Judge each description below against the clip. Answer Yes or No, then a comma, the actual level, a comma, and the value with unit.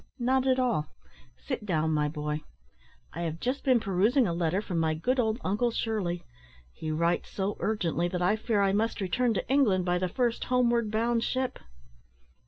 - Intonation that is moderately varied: No, wide, 5.7 semitones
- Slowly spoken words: No, average, 185 wpm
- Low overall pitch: No, high, 205 Hz